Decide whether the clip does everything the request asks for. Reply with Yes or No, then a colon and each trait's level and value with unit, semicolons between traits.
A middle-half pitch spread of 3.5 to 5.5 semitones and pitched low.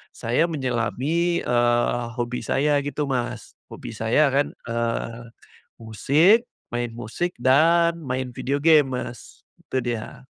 Yes: average, 3.9 semitones; low, 130 Hz